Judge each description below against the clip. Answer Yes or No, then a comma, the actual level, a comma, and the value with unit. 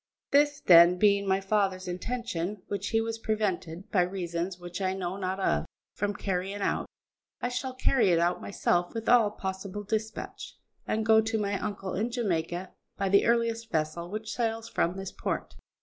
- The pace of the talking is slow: No, average, 175 wpm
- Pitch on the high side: Yes, high, 200 Hz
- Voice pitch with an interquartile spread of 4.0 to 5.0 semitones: No, average, 3.5 semitones